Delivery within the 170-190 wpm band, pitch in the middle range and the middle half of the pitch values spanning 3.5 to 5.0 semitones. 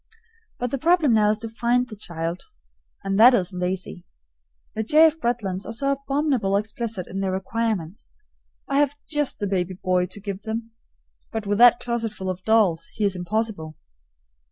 No: average, 175 wpm; high, 215 Hz; average, 4.2 semitones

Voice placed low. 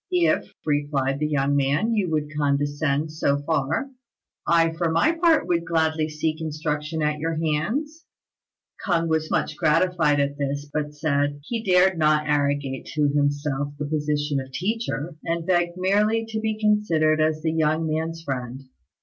No: medium, 155 Hz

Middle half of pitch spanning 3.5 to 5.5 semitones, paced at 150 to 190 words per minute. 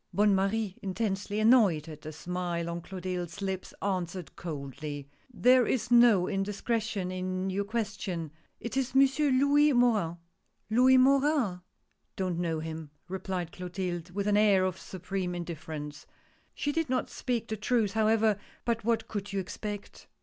Yes: average, 4.3 semitones; average, 165 wpm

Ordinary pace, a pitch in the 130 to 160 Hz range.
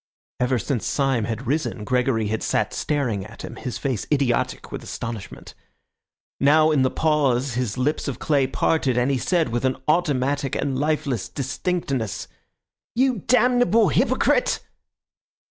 Yes: average, 145 wpm; low, 135 Hz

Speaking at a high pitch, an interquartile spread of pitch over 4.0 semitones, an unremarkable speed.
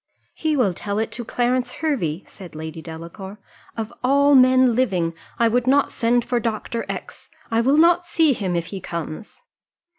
Yes: high, 230 Hz; wide, 5.6 semitones; average, 175 wpm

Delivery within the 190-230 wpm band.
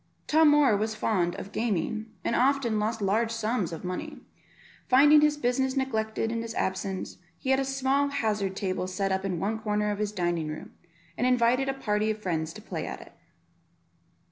Yes: average, 195 wpm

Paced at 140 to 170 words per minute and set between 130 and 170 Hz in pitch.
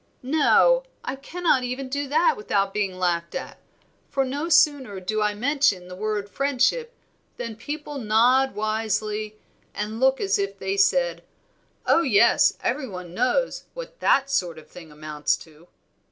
No: average, 155 wpm; high, 220 Hz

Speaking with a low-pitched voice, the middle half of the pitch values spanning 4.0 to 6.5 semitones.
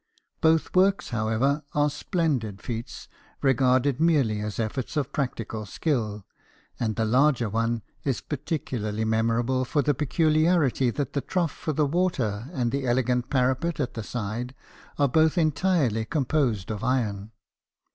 Yes: low, 130 Hz; average, 4.9 semitones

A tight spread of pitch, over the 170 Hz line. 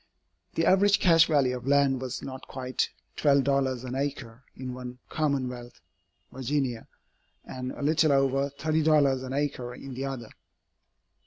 No: narrow, 2.1 semitones; low, 135 Hz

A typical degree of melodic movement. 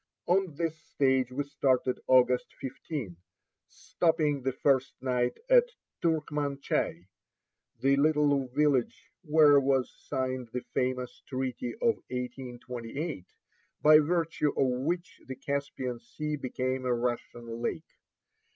Yes: average, 3.0 semitones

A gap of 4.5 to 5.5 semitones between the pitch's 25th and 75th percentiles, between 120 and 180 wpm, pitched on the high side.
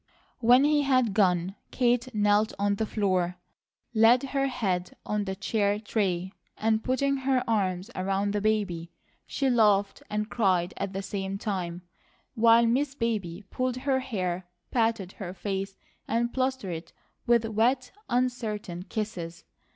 No: average, 4.1 semitones; average, 145 wpm; high, 210 Hz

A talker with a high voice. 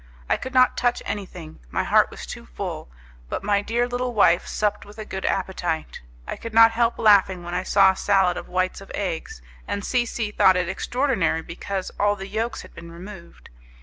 Yes: high, 195 Hz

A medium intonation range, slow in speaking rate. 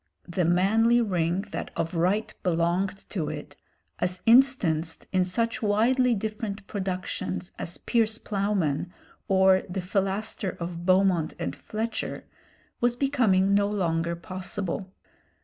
Yes: average, 3.4 semitones; slow, 120 wpm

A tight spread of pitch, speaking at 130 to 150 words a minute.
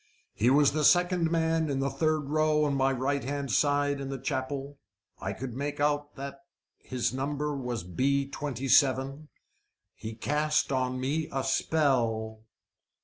Yes: narrow, 2.1 semitones; average, 145 wpm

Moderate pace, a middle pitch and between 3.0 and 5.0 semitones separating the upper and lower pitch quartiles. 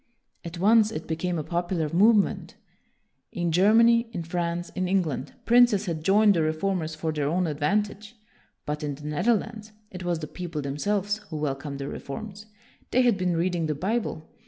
Yes: average, 180 wpm; medium, 175 Hz; average, 4.7 semitones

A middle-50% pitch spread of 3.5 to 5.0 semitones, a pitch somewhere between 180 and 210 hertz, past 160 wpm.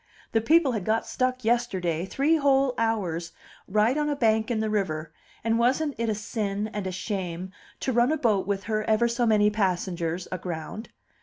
No: average, 4.2 semitones; high, 220 Hz; average, 180 wpm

